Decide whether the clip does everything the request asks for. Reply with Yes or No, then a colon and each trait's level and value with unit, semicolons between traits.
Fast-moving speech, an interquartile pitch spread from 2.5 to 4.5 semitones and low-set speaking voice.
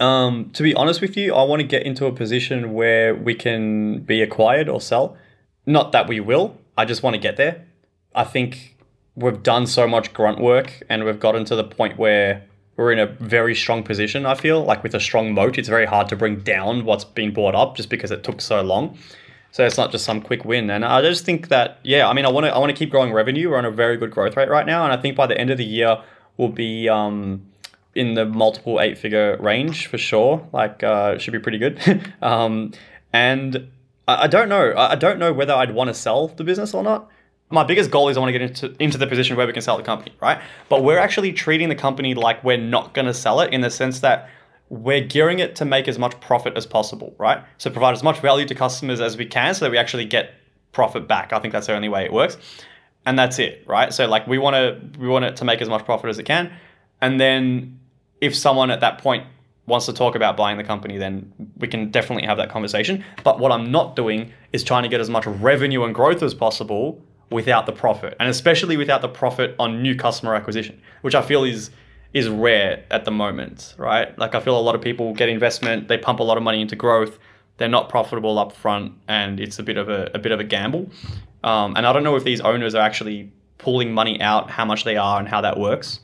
Yes: fast, 245 wpm; average, 3.3 semitones; low, 120 Hz